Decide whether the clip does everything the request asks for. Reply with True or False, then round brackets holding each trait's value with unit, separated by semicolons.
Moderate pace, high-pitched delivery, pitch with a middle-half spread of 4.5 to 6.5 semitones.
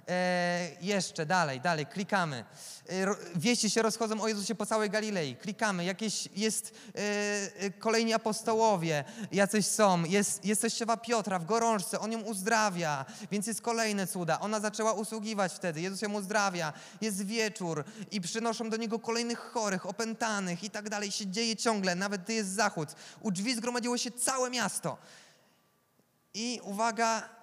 False (150 wpm; 210 Hz; 2.9 semitones)